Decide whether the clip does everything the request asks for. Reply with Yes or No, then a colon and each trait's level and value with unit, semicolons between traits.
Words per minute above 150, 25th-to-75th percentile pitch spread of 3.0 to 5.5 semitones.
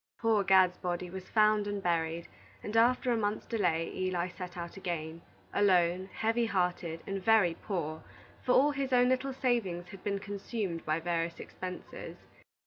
Yes: average, 160 wpm; average, 4.2 semitones